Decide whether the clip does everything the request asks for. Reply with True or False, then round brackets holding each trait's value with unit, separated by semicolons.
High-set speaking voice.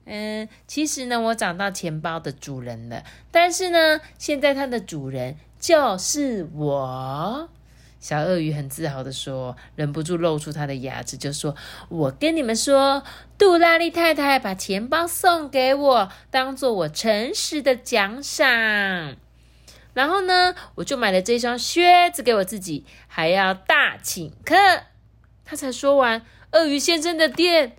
True (230 Hz)